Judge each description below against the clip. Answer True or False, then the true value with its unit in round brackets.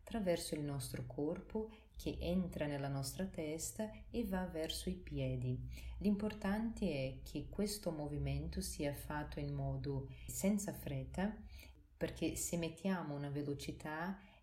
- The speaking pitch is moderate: True (160 Hz)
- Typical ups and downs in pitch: True (4.9 semitones)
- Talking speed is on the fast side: False (125 wpm)